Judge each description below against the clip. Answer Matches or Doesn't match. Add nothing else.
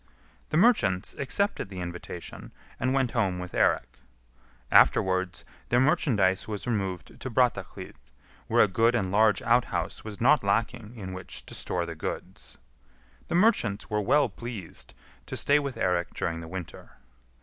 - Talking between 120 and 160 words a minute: Matches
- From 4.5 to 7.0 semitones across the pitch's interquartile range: Matches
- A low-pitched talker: Matches